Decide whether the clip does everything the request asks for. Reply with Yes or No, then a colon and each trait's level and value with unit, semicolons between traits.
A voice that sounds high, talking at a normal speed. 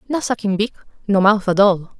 No: high, 205 Hz; fast, 210 wpm